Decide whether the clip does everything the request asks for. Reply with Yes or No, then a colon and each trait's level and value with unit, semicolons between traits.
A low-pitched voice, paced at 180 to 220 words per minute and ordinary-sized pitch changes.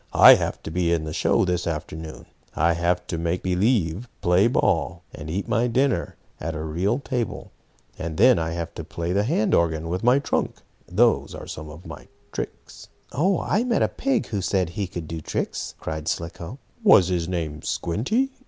No: very low, 90 Hz; average, 190 wpm; wide, 5.7 semitones